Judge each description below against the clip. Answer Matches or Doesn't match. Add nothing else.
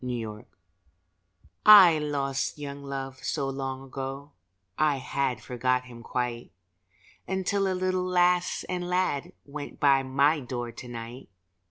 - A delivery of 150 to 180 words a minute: Doesn't match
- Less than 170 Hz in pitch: Matches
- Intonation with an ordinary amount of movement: Matches